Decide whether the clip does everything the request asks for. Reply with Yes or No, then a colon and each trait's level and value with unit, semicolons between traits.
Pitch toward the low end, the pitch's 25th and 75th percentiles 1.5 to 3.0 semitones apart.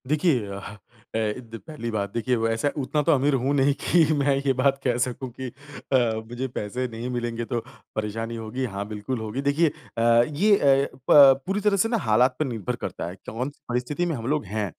No: low, 125 Hz; average, 3.9 semitones